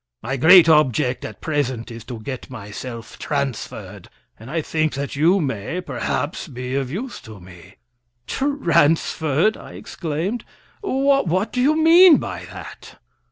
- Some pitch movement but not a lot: No, wide, 6.8 semitones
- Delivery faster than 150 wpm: No, average, 140 wpm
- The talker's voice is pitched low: No, medium, 150 Hz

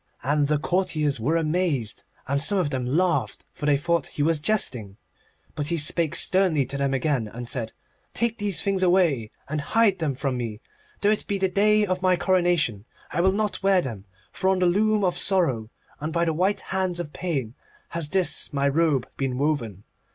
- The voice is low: No, medium, 160 Hz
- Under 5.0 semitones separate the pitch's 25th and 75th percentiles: No, average, 5.3 semitones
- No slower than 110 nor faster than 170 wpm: No, average, 200 wpm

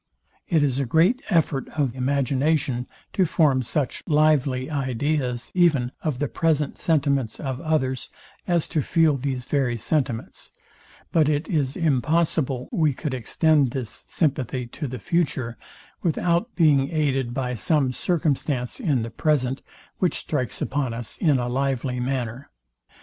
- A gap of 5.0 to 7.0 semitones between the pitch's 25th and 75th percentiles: No, average, 3.6 semitones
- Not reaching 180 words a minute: Yes, average, 140 wpm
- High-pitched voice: No, medium, 140 Hz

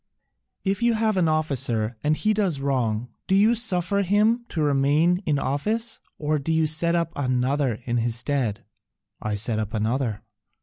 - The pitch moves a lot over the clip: Yes, wide, 7.4 semitones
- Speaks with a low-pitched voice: No, medium, 150 Hz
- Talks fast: No, average, 170 wpm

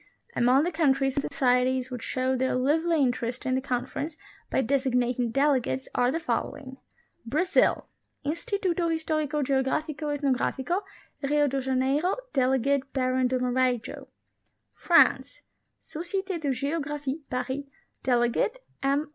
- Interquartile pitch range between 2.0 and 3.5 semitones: Yes, average, 2.8 semitones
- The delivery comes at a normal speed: No, slow, 130 wpm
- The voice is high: Yes, very high, 270 Hz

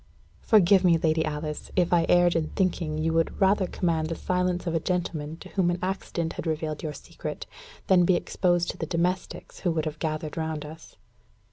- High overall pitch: No, medium, 170 Hz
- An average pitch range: No, narrow, 2.3 semitones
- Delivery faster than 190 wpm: Yes, average, 200 wpm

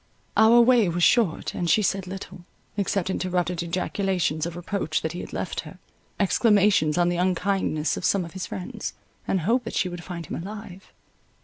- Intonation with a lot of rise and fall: No, narrow, 2.5 semitones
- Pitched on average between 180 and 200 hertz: Yes, medium, 185 Hz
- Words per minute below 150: No, average, 185 wpm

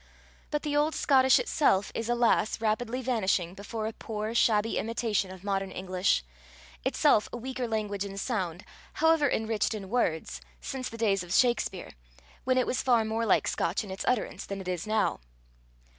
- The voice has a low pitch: No, high, 220 Hz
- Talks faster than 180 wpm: No, average, 175 wpm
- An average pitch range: Yes, average, 3.9 semitones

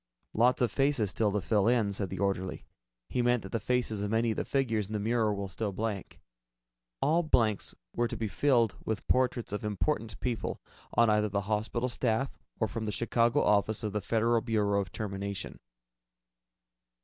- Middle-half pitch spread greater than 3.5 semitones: No, average, 2.7 semitones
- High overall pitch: No, low, 110 Hz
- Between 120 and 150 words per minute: No, average, 185 wpm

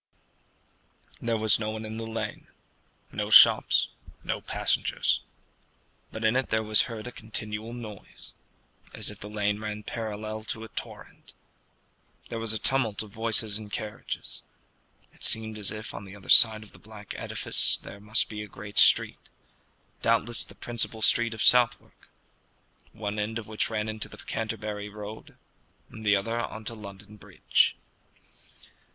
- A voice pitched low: Yes, low, 110 Hz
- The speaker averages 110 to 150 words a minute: No, average, 160 wpm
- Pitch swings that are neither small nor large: No, narrow, 1.1 semitones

